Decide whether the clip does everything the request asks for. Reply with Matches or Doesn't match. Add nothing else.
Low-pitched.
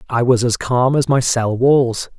Matches